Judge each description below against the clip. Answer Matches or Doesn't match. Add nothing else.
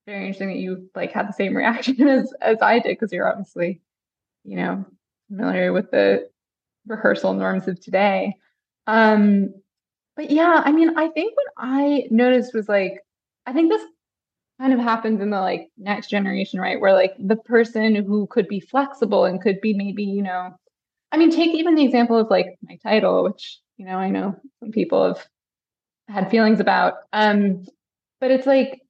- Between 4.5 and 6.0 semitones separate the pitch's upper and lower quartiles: Matches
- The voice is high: Matches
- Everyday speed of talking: Matches